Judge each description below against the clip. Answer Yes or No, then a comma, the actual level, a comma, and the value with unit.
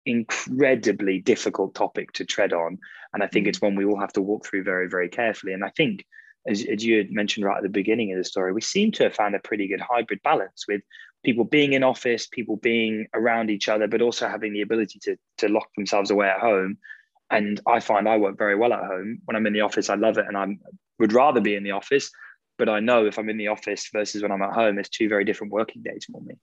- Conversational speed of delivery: No, fast, 255 wpm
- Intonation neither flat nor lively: No, narrow, 2.3 semitones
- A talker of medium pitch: No, low, 105 Hz